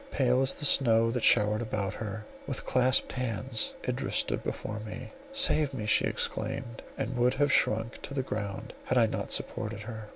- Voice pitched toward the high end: No, low, 115 Hz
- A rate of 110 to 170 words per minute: No, average, 185 wpm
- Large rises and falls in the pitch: No, average, 3.2 semitones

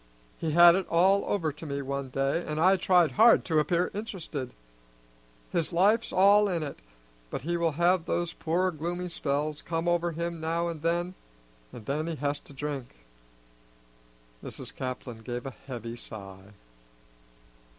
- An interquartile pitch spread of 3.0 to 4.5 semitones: Yes, average, 3.7 semitones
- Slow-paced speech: No, average, 160 wpm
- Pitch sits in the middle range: Yes, medium, 165 Hz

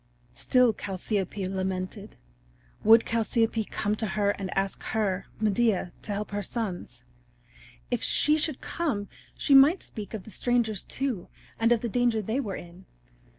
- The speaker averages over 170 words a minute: No, average, 150 wpm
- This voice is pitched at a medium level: No, high, 215 Hz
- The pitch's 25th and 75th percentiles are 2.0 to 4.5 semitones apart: Yes, average, 3.4 semitones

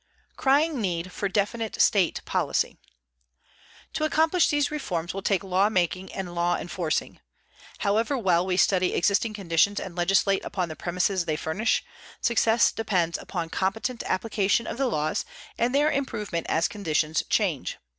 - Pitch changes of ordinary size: Yes, average, 4.5 semitones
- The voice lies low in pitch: No, high, 195 Hz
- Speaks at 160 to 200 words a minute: No, average, 150 wpm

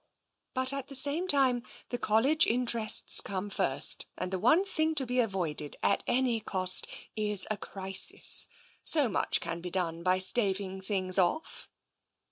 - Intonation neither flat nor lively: No, wide, 5.7 semitones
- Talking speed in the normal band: Yes, average, 160 wpm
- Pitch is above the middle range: Yes, high, 210 Hz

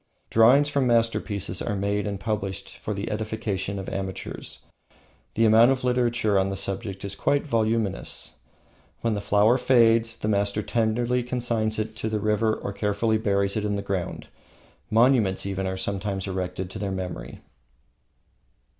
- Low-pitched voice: Yes, low, 105 Hz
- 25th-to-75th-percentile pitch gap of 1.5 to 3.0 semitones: Yes, narrow, 2.6 semitones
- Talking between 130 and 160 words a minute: Yes, average, 155 wpm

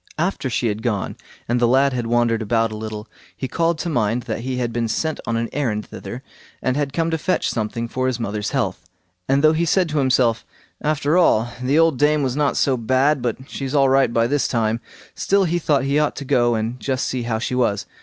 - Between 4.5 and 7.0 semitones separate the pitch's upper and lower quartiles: No, average, 4.0 semitones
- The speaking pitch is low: Yes, low, 130 Hz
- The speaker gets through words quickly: Yes, fast, 230 wpm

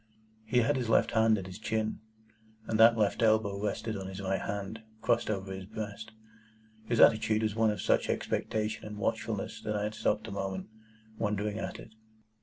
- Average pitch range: No, narrow, 1.8 semitones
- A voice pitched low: Yes, low, 110 Hz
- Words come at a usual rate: Yes, average, 185 wpm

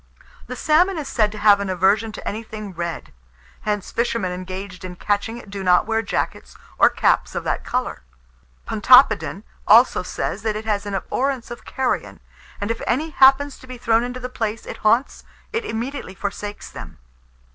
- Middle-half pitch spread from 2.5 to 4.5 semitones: Yes, average, 3.8 semitones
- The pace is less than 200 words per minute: Yes, average, 180 wpm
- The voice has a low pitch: No, high, 220 Hz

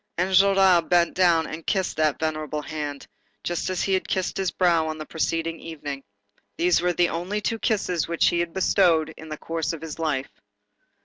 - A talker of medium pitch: Yes, medium, 165 Hz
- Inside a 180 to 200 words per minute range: Yes, average, 190 wpm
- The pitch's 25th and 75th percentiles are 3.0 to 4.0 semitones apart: No, narrow, 2.6 semitones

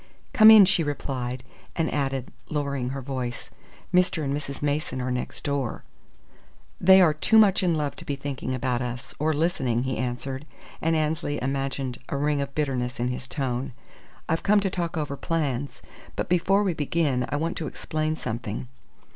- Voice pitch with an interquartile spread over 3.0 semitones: Yes, average, 3.8 semitones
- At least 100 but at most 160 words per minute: No, average, 175 wpm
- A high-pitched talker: No, medium, 140 Hz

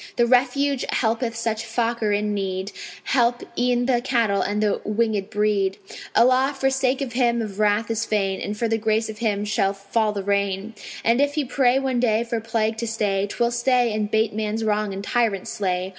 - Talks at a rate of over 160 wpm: Yes, average, 200 wpm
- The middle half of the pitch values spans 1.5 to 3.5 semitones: Yes, average, 2.7 semitones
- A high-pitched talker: Yes, high, 225 Hz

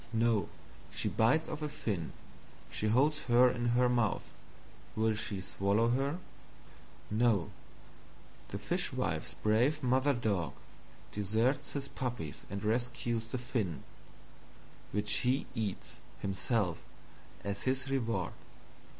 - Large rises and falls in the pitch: No, average, 3.6 semitones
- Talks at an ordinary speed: No, slow, 115 wpm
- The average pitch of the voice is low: Yes, low, 115 Hz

